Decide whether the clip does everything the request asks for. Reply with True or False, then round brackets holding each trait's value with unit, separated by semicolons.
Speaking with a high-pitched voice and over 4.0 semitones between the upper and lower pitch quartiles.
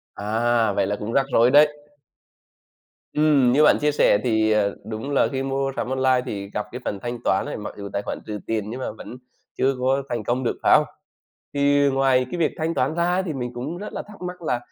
False (130 Hz; 4.4 semitones)